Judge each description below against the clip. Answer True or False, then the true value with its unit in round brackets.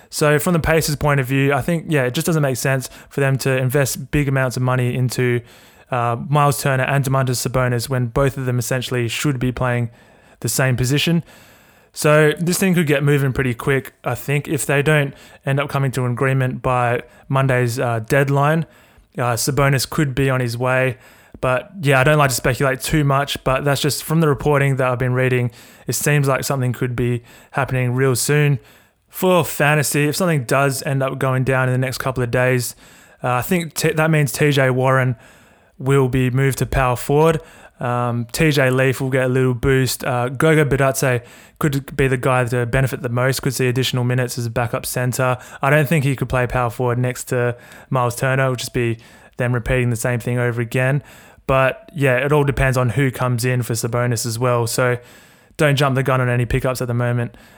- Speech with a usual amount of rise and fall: False (2.1 semitones)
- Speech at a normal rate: False (210 wpm)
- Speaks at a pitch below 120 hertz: False (130 Hz)